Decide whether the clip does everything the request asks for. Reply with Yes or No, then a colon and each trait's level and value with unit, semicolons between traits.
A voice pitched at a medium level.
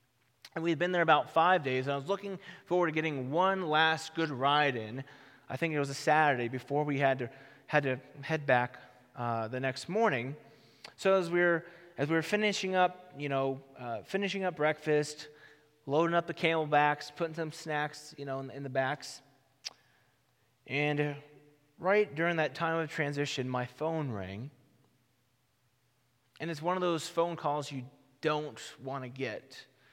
Yes: medium, 150 Hz